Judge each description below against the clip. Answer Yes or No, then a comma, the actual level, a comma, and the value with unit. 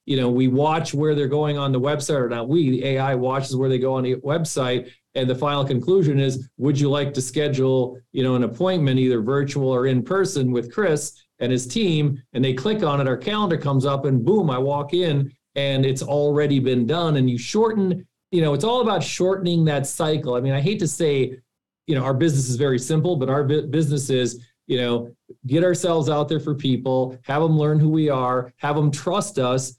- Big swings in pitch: No, average, 3.3 semitones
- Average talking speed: No, fast, 225 wpm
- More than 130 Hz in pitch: Yes, medium, 140 Hz